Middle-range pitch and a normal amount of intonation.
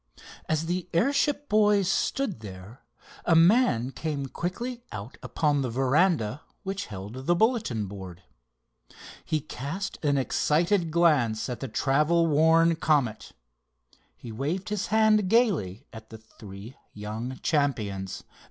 No: medium, 150 Hz; wide, 8.3 semitones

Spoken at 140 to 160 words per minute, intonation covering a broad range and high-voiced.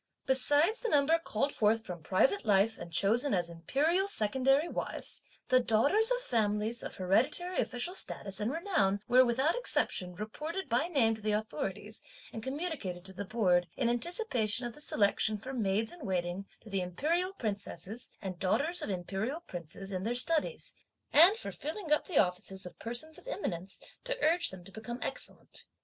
No: average, 175 wpm; wide, 7.9 semitones; high, 230 Hz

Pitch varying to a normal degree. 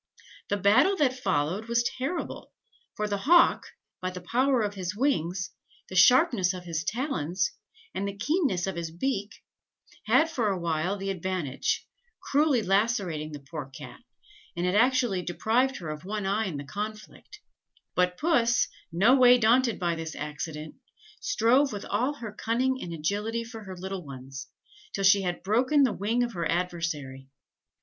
No: wide, 5.8 semitones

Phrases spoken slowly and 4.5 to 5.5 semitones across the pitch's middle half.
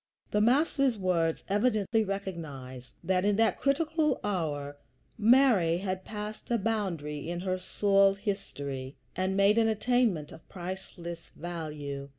Yes: slow, 130 wpm; average, 4.8 semitones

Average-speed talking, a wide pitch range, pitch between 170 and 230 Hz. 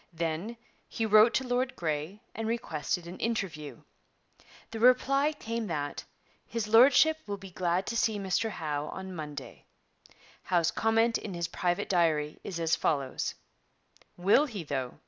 Yes: average, 145 wpm; wide, 6.0 semitones; high, 190 Hz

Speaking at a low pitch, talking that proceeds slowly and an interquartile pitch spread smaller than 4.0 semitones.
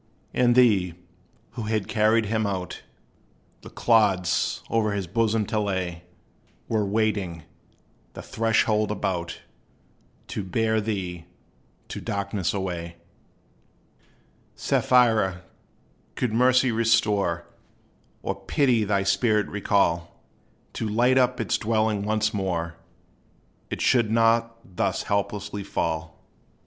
Yes: low, 105 Hz; slow, 105 wpm; average, 3.1 semitones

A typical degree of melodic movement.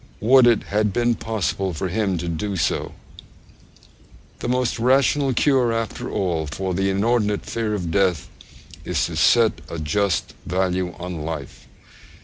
Yes: average, 4.6 semitones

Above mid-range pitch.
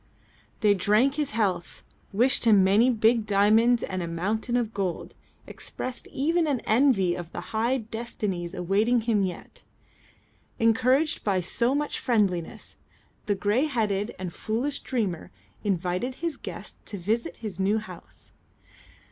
Yes: high, 215 Hz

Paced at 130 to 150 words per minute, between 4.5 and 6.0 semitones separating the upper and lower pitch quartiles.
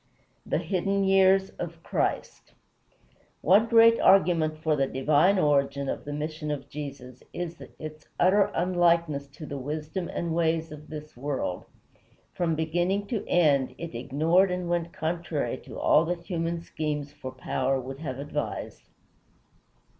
No: average, 145 wpm; average, 3.4 semitones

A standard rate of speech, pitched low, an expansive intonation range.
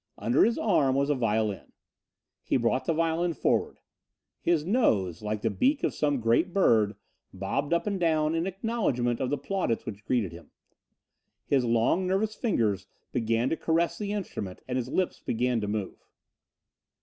Yes: average, 165 wpm; low, 130 Hz; wide, 7.5 semitones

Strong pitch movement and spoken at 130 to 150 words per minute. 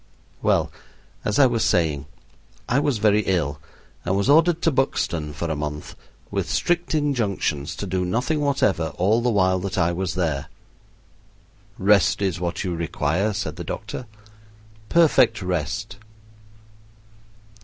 Yes: wide, 6.5 semitones; average, 140 wpm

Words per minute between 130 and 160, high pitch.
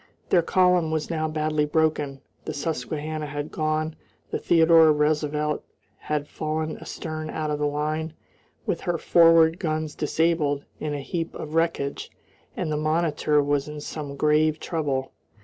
No: average, 150 wpm; medium, 155 Hz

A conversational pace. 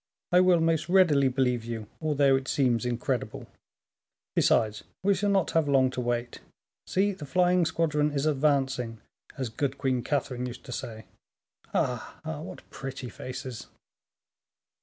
Yes: average, 145 wpm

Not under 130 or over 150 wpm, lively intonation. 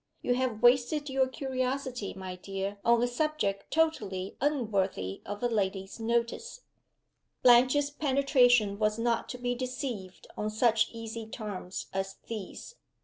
No: slow, 135 wpm; average, 4.4 semitones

